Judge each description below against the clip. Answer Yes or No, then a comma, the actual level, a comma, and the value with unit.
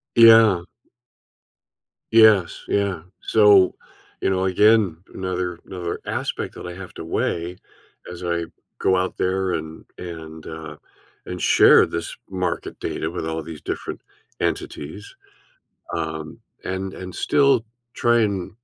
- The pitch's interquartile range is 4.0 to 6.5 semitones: No, average, 3.1 semitones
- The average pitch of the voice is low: Yes, very low, 90 Hz